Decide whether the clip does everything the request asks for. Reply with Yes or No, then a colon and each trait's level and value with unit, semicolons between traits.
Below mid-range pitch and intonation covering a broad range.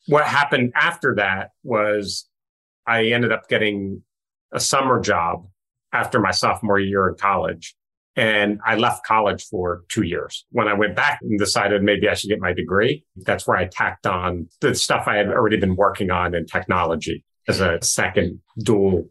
No: low, 100 Hz; average, 3.4 semitones